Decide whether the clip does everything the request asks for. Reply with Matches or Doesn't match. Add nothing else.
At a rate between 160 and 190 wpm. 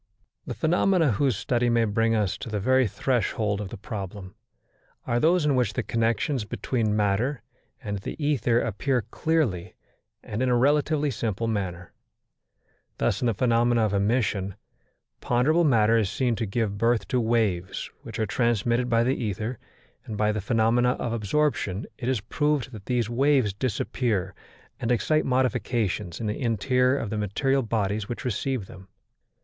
Matches